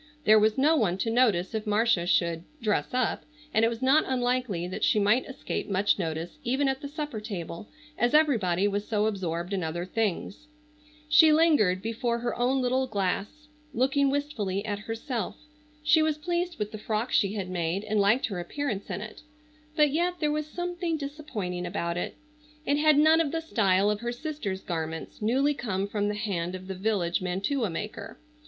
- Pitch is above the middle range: Yes, high, 220 Hz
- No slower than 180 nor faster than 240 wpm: Yes, average, 190 wpm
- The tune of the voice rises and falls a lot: Yes, wide, 6.6 semitones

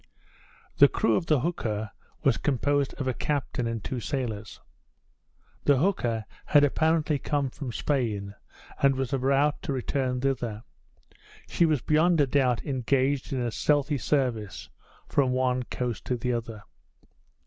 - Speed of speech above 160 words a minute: No, average, 145 wpm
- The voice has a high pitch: No, low, 130 Hz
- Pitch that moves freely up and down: No, average, 3.2 semitones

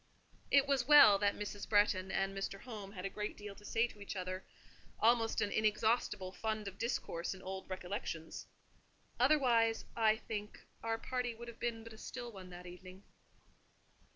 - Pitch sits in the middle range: No, high, 210 Hz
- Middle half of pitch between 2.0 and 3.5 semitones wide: Yes, average, 3.1 semitones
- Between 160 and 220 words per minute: Yes, average, 170 wpm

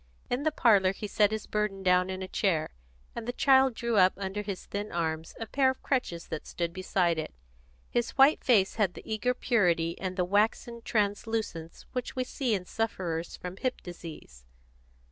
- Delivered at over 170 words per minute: Yes, average, 185 wpm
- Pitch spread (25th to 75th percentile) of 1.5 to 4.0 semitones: No, average, 4.6 semitones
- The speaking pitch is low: No, high, 200 Hz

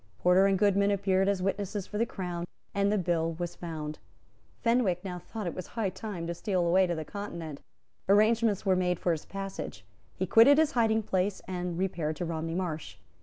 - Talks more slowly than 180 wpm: No, average, 200 wpm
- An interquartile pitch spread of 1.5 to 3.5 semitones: Yes, average, 2.9 semitones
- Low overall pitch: No, medium, 185 Hz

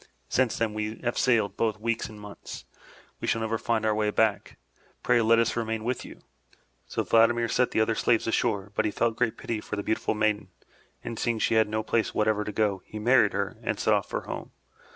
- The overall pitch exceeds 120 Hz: No, low, 110 Hz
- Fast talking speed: Yes, fast, 220 wpm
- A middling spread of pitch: No, narrow, 1.4 semitones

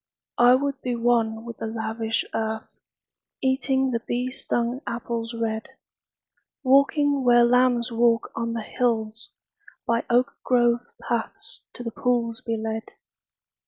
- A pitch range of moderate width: No, narrow, 1.7 semitones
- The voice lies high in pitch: Yes, high, 235 Hz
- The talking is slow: Yes, slow, 130 wpm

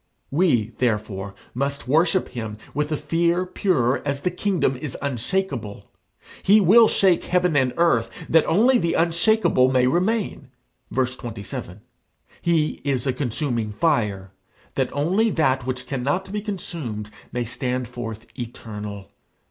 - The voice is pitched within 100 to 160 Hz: Yes, medium, 140 Hz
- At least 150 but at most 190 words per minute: No, slow, 135 wpm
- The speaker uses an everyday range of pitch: No, wide, 6.2 semitones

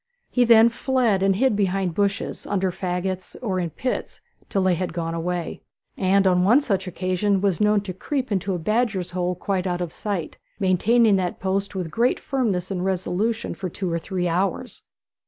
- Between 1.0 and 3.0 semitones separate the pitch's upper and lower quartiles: Yes, narrow, 2.6 semitones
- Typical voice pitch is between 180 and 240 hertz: Yes, high, 190 Hz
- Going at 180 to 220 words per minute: Yes, average, 185 wpm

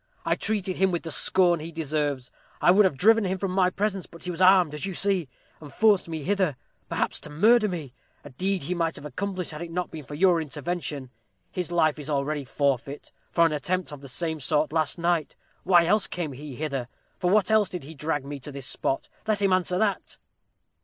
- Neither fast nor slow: No, fast, 220 wpm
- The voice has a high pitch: No, medium, 170 Hz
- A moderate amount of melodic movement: Yes, average, 4.0 semitones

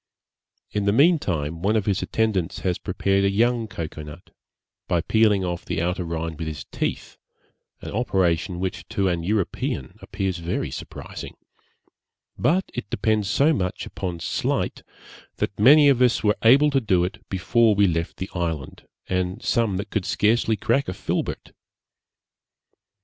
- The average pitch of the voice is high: No, very low, 95 Hz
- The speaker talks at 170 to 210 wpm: No, average, 155 wpm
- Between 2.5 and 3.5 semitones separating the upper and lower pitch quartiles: No, average, 4.2 semitones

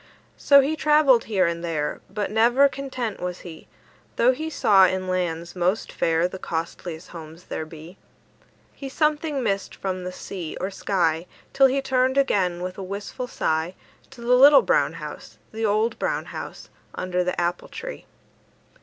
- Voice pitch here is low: No, high, 195 Hz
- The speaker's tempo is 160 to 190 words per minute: Yes, average, 165 wpm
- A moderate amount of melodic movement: No, wide, 6.7 semitones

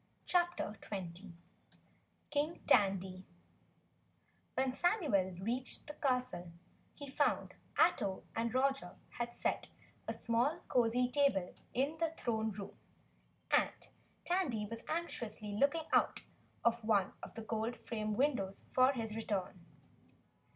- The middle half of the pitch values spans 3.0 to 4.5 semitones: No, average, 5.3 semitones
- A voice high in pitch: Yes, high, 235 Hz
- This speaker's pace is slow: Yes, slow, 115 wpm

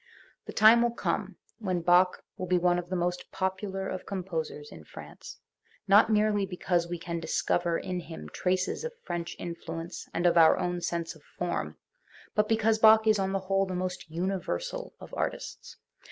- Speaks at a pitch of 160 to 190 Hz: Yes, medium, 185 Hz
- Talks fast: No, average, 180 wpm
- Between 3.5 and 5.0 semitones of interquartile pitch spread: No, average, 2.8 semitones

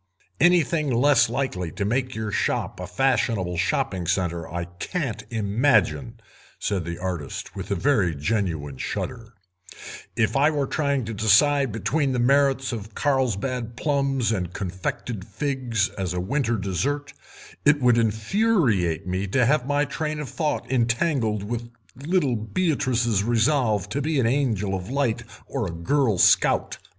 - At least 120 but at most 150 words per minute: Yes, average, 145 wpm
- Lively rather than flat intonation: Yes, wide, 5.9 semitones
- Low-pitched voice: Yes, low, 115 Hz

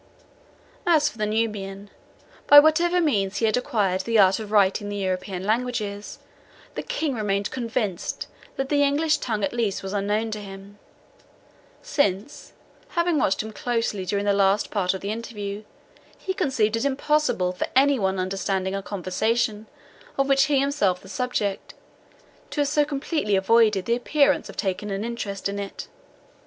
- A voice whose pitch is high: Yes, high, 215 Hz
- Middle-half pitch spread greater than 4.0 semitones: Yes, wide, 5.5 semitones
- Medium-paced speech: Yes, average, 165 wpm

